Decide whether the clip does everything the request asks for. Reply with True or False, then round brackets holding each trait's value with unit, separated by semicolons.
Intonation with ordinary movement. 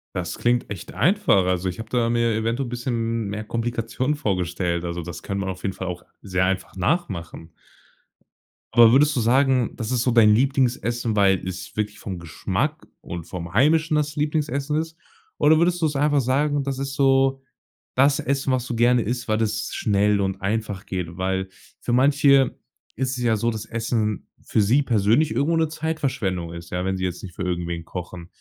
False (6.2 semitones)